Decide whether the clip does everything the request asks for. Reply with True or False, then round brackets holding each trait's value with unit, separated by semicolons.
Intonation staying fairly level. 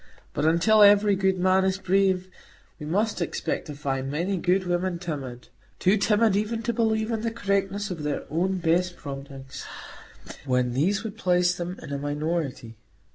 False (5.1 semitones)